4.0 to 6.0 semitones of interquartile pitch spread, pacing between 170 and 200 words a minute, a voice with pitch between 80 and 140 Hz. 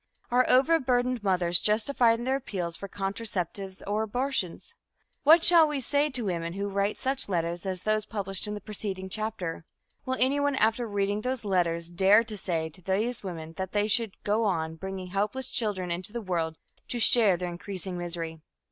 No: average, 4.6 semitones; average, 180 wpm; high, 205 Hz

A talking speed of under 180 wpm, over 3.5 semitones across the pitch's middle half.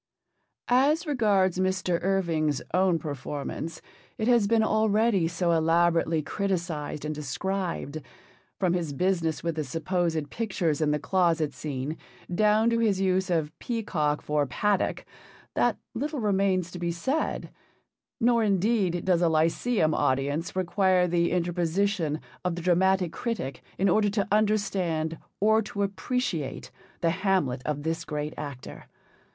Yes: slow, 135 wpm; average, 4.1 semitones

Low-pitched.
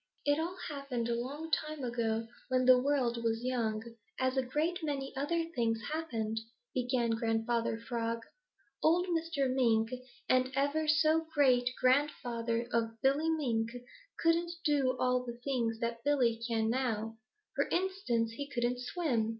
No: very high, 255 Hz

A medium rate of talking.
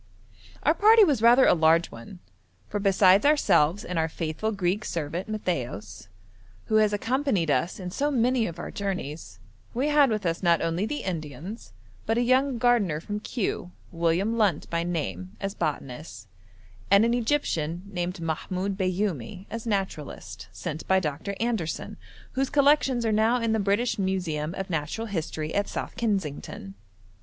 Yes: average, 160 wpm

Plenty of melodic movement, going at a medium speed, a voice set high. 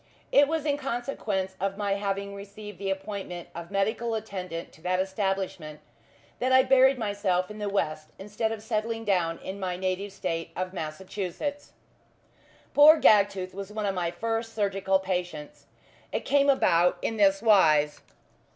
No: average, 3.1 semitones; average, 155 wpm; high, 195 Hz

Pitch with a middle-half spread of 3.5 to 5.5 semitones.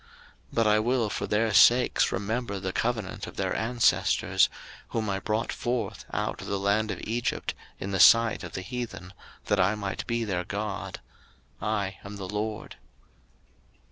No: narrow, 2.5 semitones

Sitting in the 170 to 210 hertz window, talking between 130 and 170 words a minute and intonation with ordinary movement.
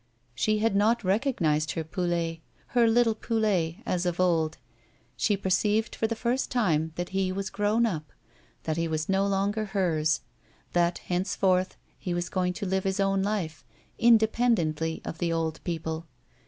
Yes: medium, 185 Hz; average, 160 wpm; average, 4.4 semitones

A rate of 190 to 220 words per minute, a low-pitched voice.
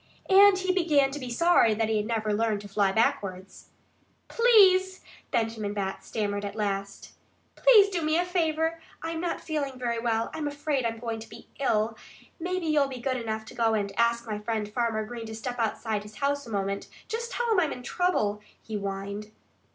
No: average, 200 wpm; high, 235 Hz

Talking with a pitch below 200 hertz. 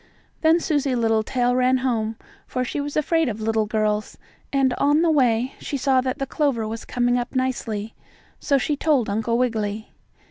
No: very high, 250 Hz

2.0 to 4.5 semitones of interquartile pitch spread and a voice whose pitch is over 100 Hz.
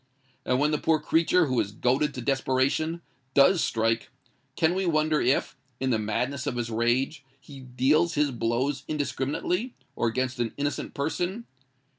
Yes: average, 4.0 semitones; medium, 140 Hz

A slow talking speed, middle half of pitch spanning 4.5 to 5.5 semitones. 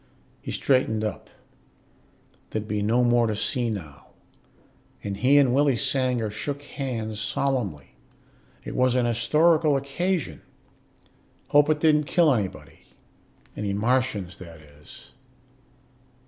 Yes: slow, 120 wpm; average, 4.9 semitones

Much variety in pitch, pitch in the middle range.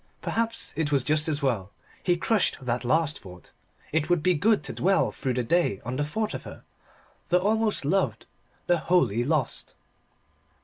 Yes: wide, 5.9 semitones; medium, 155 Hz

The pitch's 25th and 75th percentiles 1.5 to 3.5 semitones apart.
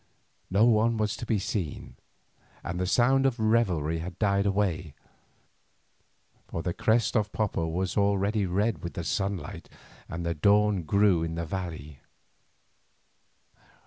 No: average, 4.0 semitones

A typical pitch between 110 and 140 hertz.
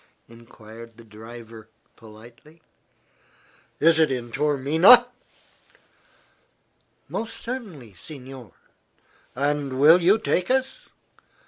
Yes: low, 135 Hz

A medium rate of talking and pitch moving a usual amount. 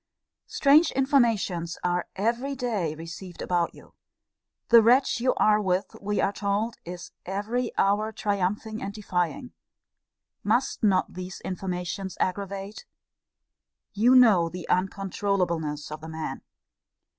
No: slow, 120 wpm; average, 3.8 semitones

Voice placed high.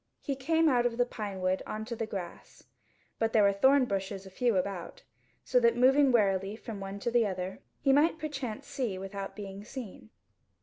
Yes: high, 220 Hz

